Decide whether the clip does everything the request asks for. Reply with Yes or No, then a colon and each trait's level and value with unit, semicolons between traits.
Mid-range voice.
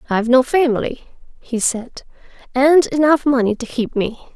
No: very high, 255 Hz